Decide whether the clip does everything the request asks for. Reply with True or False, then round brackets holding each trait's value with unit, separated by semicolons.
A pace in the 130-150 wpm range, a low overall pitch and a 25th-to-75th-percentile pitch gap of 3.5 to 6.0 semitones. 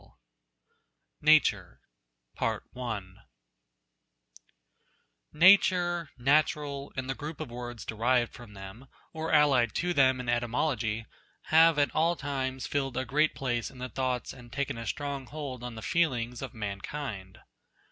True (135 wpm; 130 Hz; 3.8 semitones)